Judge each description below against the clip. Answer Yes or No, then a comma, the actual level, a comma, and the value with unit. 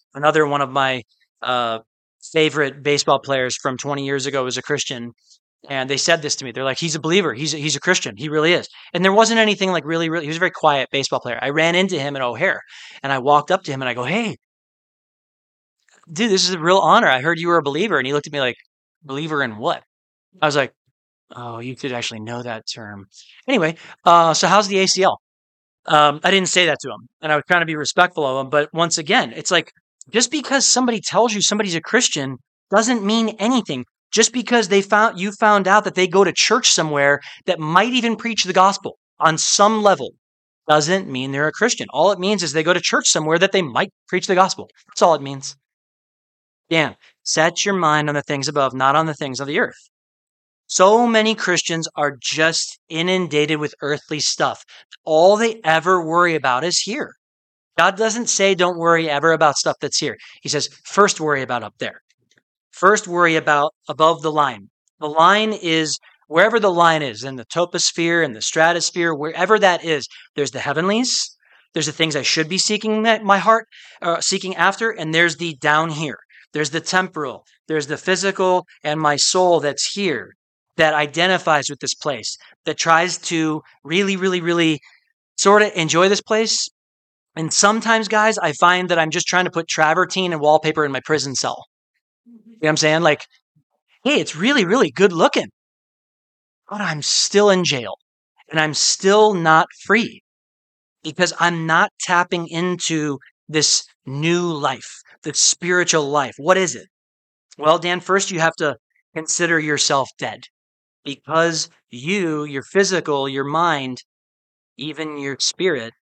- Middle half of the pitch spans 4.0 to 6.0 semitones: Yes, average, 4.5 semitones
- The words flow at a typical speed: Yes, average, 190 wpm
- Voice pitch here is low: No, medium, 160 Hz